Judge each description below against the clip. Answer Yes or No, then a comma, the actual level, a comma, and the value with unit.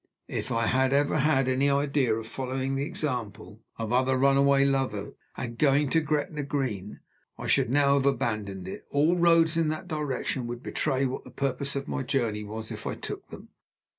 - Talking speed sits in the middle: Yes, average, 190 wpm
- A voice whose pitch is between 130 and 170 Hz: Yes, low, 135 Hz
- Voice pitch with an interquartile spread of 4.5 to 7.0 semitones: No, average, 3.3 semitones